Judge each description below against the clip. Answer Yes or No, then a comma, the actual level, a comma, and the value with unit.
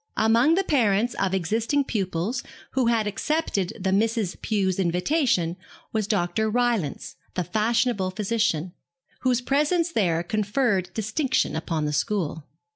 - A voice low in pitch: No, high, 215 Hz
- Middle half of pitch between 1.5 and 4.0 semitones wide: No, average, 4.7 semitones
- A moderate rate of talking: No, slow, 125 wpm